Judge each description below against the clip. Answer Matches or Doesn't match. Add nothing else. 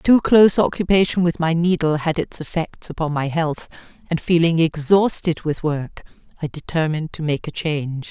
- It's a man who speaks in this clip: Doesn't match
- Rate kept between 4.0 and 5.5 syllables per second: Matches